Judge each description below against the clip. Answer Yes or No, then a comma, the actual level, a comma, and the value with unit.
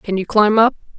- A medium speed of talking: No, fast, 245 wpm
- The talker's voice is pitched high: Yes, high, 210 Hz